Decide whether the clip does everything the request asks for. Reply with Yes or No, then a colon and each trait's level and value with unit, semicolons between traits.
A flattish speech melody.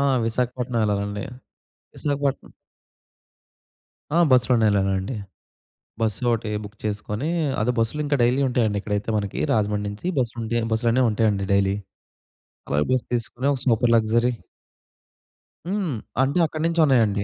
No: average, 3.6 semitones